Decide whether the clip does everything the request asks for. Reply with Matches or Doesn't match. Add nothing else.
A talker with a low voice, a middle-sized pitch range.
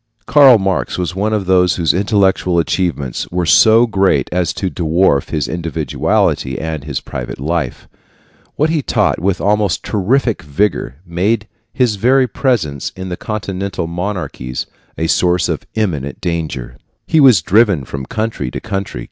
Matches